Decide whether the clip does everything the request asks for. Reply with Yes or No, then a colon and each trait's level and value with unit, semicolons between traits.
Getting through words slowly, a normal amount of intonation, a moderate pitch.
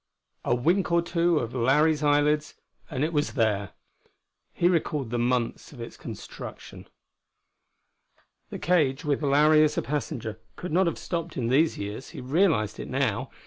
No: average, 160 wpm; average, 4.7 semitones; medium, 145 Hz